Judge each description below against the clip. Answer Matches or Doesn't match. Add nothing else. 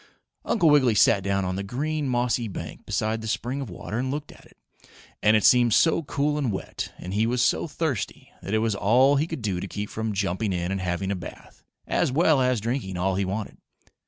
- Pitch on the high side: Doesn't match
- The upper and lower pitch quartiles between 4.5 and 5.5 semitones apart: Matches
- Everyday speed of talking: Doesn't match